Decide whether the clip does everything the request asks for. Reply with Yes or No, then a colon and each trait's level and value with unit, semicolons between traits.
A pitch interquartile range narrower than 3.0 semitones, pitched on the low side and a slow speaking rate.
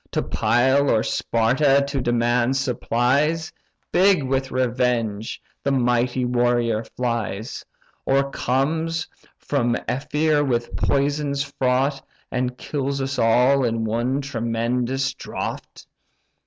Yes: narrow, 2.5 semitones; low, 130 Hz; slow, 105 wpm